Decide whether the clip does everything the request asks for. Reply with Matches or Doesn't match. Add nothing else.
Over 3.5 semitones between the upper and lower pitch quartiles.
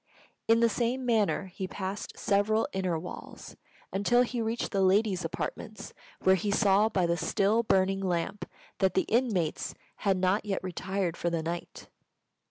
Doesn't match